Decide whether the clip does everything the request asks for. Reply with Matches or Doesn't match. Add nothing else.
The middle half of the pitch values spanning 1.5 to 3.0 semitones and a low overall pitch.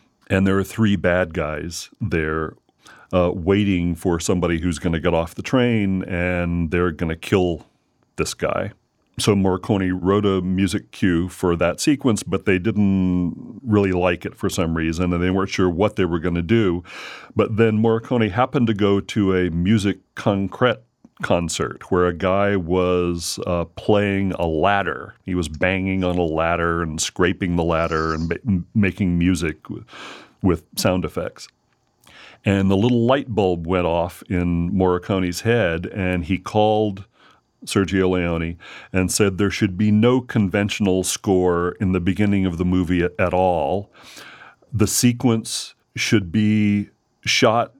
Matches